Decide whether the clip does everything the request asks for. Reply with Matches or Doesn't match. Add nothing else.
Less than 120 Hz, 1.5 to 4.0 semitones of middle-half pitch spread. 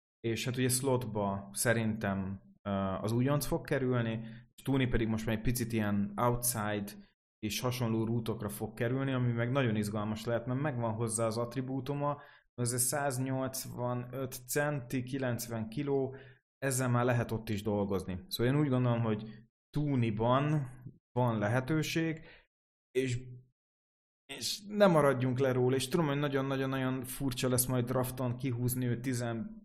Doesn't match